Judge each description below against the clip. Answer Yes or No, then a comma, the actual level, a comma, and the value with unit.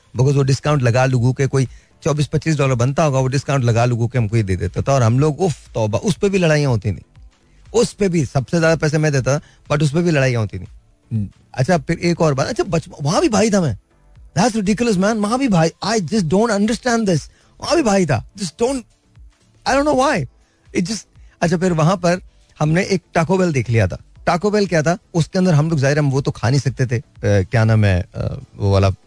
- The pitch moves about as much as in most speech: No, wide, 6.4 semitones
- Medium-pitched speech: Yes, medium, 150 Hz